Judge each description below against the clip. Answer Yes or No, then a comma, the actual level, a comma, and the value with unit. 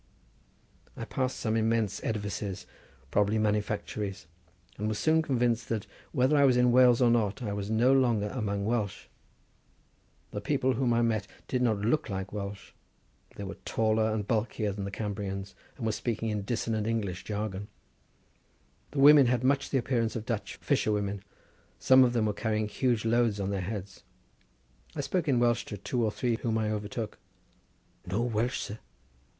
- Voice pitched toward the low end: Yes, low, 110 Hz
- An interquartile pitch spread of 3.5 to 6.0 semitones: No, average, 2.8 semitones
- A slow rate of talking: No, average, 170 wpm